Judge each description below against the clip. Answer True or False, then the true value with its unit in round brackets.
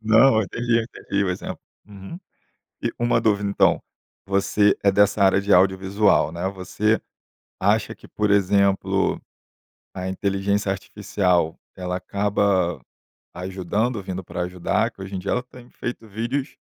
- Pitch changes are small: True (2.3 semitones)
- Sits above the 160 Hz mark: False (100 Hz)